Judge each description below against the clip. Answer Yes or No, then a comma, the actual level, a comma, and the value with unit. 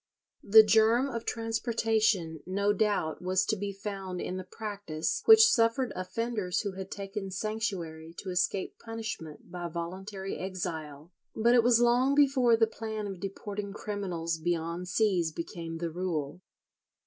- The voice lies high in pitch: Yes, high, 195 Hz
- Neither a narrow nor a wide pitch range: Yes, average, 4.2 semitones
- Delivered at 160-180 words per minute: No, average, 145 wpm